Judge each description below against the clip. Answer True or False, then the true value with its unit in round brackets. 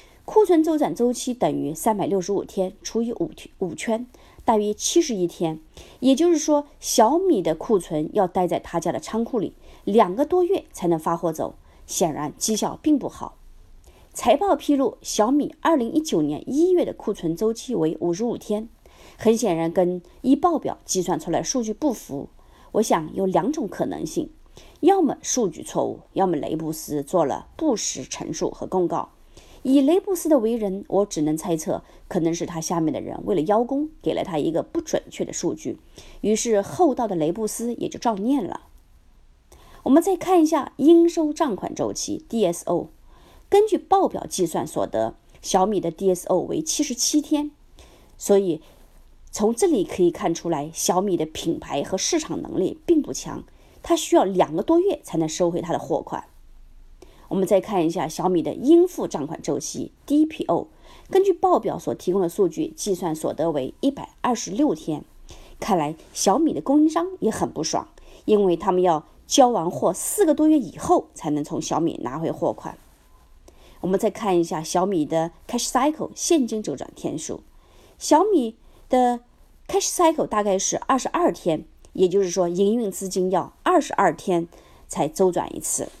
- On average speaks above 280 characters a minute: False (265 characters per minute)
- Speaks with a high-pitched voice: True (220 Hz)